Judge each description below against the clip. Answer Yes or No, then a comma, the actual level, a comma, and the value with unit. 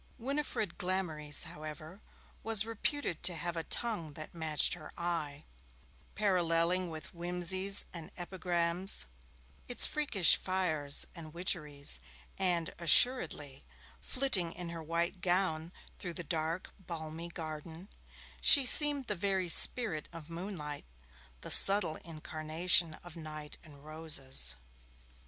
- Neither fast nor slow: No, slow, 115 wpm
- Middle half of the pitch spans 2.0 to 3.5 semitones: Yes, average, 3.2 semitones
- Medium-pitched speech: Yes, medium, 170 Hz